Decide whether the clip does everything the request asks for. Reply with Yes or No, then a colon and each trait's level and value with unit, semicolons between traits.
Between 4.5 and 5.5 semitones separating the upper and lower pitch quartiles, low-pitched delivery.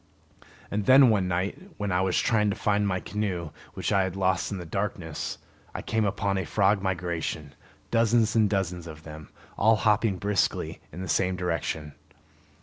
No: average, 2.9 semitones; very low, 95 Hz